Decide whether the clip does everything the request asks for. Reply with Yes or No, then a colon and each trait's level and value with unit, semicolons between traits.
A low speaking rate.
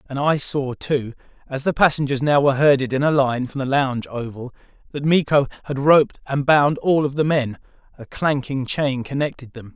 No: average, 195 wpm